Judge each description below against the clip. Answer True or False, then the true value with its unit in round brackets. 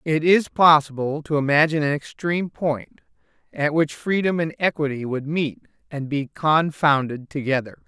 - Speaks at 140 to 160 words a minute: True (145 wpm)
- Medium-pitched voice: True (150 Hz)